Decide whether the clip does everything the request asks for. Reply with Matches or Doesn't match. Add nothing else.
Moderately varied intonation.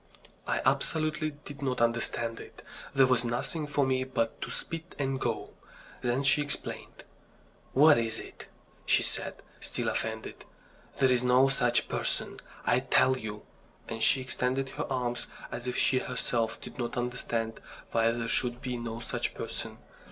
Doesn't match